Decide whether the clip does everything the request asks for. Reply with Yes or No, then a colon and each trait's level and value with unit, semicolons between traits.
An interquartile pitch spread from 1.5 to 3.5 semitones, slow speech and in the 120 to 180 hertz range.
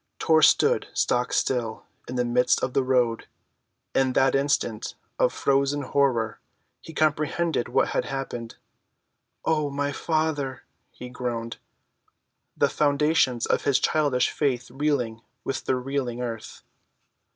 Yes: average, 2.8 semitones; slow, 125 wpm; low, 135 Hz